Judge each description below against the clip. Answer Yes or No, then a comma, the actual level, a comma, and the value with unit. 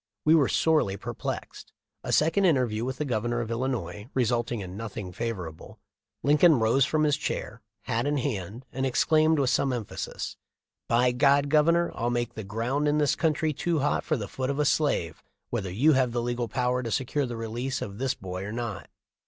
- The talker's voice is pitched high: No, low, 125 Hz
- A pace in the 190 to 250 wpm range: Yes, average, 195 wpm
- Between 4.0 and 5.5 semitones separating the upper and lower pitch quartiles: Yes, average, 4.3 semitones